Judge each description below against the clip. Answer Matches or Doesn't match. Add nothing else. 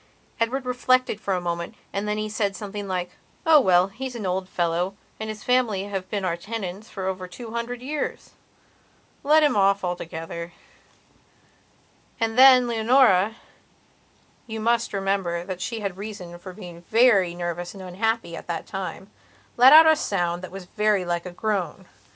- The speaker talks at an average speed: Matches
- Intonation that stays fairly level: Doesn't match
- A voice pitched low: Doesn't match